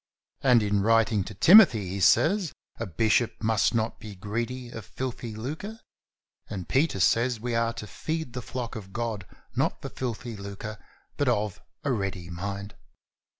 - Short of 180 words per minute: Yes, average, 160 wpm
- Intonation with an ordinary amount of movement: Yes, average, 3.5 semitones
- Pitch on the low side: Yes, low, 115 Hz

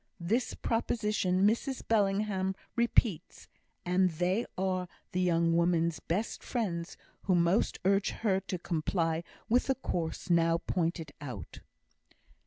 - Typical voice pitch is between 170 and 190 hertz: Yes, medium, 185 Hz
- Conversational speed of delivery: No, slow, 120 wpm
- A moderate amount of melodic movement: Yes, average, 3.8 semitones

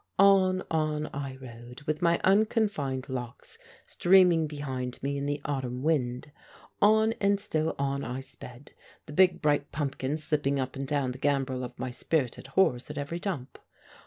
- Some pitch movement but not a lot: Yes, average, 3.9 semitones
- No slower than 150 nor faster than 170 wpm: Yes, average, 160 wpm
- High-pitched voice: No, medium, 145 Hz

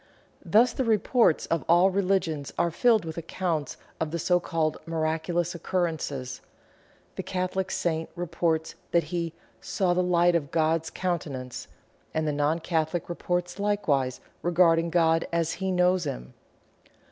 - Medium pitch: Yes, medium, 170 Hz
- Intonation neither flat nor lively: No, narrow, 2.2 semitones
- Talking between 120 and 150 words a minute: Yes, average, 140 wpm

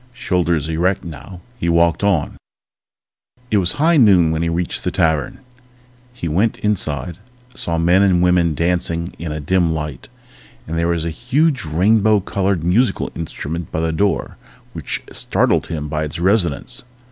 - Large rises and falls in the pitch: No, average, 3.5 semitones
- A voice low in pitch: Yes, very low, 85 Hz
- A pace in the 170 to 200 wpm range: No, average, 160 wpm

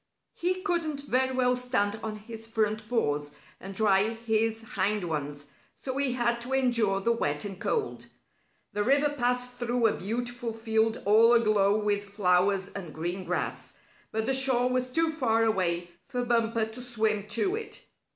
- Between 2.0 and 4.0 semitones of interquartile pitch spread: Yes, average, 3.5 semitones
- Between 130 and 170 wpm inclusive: Yes, average, 165 wpm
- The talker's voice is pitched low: No, high, 225 Hz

